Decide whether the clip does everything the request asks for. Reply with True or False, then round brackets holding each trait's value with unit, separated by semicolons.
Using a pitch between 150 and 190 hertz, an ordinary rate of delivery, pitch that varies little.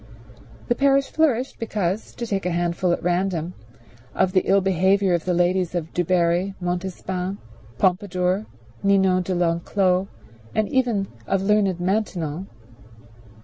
False (185 Hz; 130 wpm; 2.0 semitones)